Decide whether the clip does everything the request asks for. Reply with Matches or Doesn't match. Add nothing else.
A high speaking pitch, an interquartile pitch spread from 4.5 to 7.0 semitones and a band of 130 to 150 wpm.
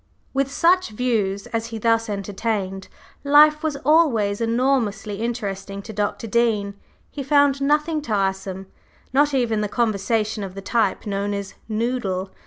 Matches